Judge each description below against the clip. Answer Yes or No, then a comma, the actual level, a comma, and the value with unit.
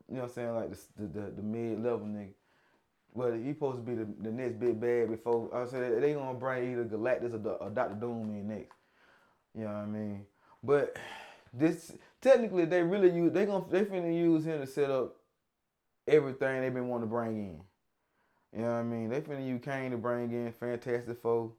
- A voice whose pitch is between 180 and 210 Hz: No, low, 120 Hz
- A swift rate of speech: Yes, fast, 215 wpm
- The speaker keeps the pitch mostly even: No, average, 3.2 semitones